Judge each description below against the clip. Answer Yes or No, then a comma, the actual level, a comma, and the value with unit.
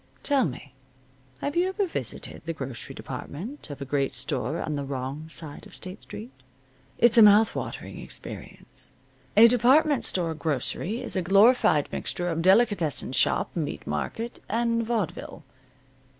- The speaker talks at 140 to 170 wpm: Yes, average, 150 wpm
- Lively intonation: Yes, wide, 8.0 semitones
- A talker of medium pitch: Yes, medium, 180 Hz